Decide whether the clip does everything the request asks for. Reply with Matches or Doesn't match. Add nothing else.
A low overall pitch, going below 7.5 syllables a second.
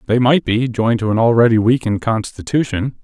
Matches